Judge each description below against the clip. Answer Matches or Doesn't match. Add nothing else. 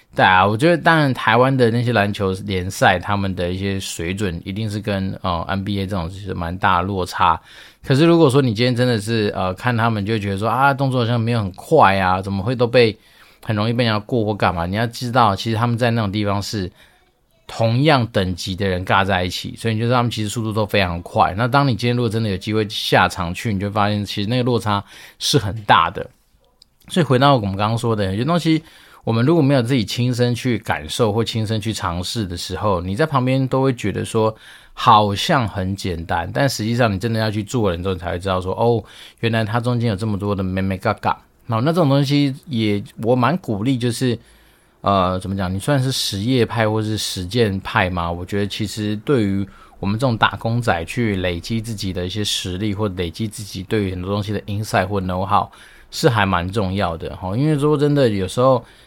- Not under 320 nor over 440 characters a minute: Matches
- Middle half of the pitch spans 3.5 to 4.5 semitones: Matches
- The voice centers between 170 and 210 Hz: Doesn't match